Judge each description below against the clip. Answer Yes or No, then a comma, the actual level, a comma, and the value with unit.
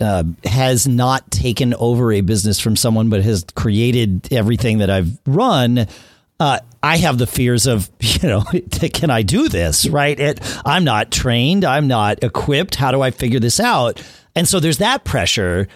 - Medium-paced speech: Yes, average, 180 wpm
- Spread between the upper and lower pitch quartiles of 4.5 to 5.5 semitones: No, average, 4.1 semitones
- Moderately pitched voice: No, low, 120 Hz